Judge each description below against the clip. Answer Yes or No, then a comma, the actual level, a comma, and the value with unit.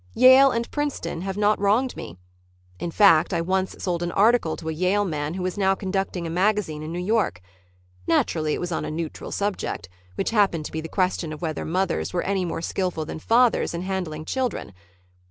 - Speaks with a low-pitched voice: No, medium, 185 Hz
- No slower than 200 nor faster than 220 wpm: Yes, fast, 205 wpm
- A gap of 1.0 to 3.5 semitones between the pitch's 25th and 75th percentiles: No, average, 4.0 semitones